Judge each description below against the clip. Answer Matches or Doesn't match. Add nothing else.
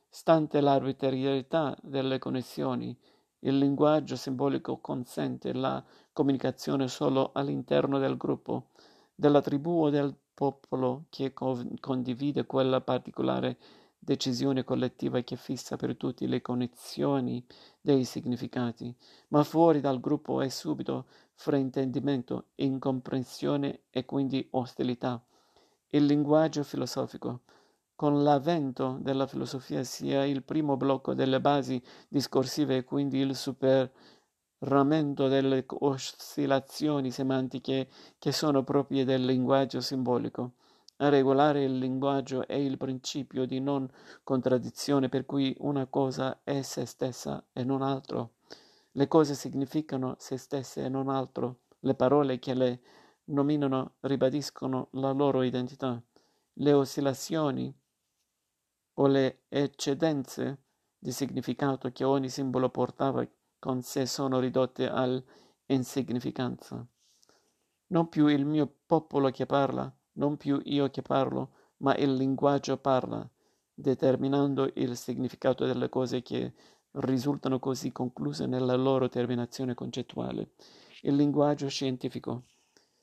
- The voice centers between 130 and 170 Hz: Matches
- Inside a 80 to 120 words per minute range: Matches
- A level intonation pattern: Matches